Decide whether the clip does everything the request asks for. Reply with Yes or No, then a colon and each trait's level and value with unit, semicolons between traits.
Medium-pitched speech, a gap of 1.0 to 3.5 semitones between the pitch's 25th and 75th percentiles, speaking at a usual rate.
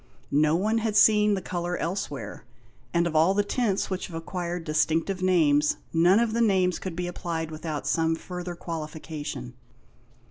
Yes: medium, 175 Hz; average, 3.0 semitones; average, 165 wpm